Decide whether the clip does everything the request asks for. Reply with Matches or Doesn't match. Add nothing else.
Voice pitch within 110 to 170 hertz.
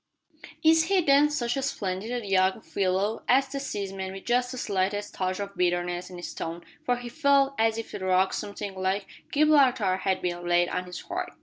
Doesn't match